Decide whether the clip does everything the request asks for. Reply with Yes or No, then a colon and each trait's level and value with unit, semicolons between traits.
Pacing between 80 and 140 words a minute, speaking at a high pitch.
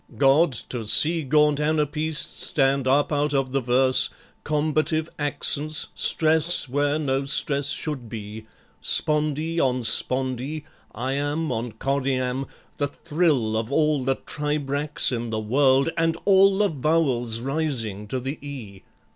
No: slow, 135 wpm; medium, 140 Hz